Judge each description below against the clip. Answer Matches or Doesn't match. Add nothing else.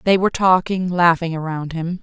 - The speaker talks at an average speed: Matches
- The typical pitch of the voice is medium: Matches